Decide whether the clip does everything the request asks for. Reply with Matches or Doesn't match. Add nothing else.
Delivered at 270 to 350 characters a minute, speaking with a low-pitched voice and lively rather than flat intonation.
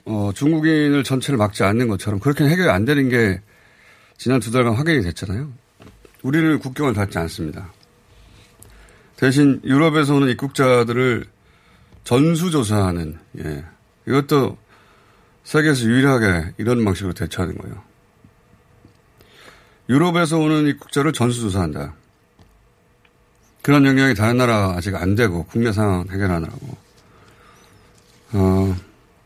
Matches